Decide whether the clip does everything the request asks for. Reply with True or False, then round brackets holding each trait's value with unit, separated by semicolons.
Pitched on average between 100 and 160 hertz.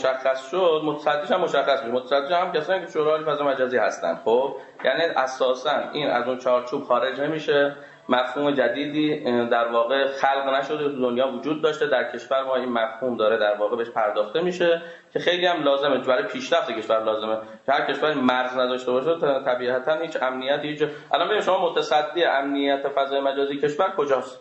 True (135 Hz)